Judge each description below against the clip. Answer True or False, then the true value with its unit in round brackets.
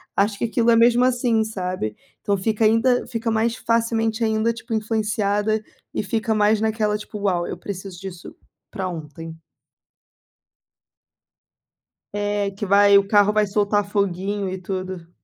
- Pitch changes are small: True (2.3 semitones)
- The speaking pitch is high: True (210 Hz)